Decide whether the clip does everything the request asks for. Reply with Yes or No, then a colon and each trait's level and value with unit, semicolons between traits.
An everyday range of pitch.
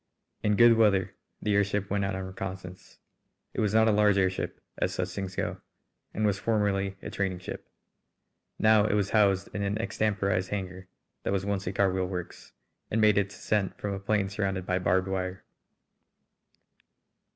No: narrow, 1.6 semitones